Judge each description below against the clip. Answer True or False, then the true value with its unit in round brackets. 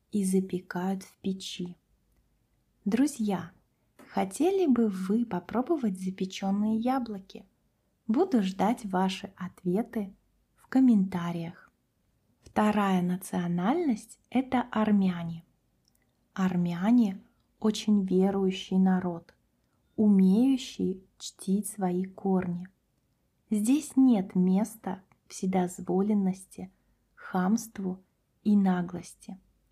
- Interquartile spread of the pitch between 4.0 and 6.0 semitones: False (2.8 semitones)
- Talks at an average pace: False (75 wpm)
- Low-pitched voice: False (195 Hz)